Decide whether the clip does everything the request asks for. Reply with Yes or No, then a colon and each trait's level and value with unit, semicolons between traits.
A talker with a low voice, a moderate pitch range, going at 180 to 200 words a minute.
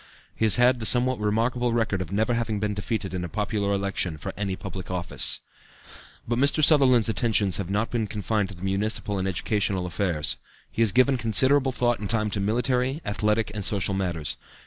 Yes: low, 105 Hz; average, 3.5 semitones; average, 190 wpm